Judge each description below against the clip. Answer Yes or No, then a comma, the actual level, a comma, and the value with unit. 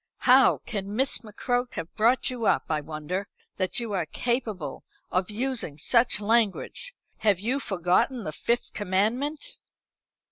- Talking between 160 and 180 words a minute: No, average, 140 wpm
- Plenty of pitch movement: No, average, 4.8 semitones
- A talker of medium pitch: No, high, 215 Hz